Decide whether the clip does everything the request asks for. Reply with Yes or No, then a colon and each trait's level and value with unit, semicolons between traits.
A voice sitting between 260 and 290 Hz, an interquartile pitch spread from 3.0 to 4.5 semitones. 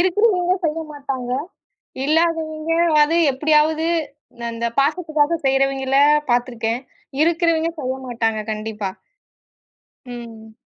No: very high, 280 Hz; average, 5.0 semitones